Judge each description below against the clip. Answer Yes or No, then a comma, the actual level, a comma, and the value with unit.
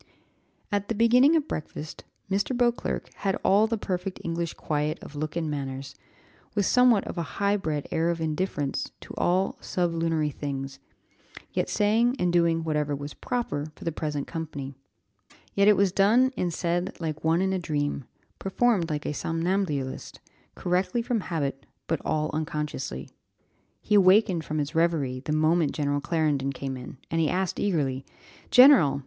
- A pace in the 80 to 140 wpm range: No, average, 160 wpm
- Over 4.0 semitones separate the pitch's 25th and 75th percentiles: Yes, average, 4.7 semitones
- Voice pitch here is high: No, medium, 165 Hz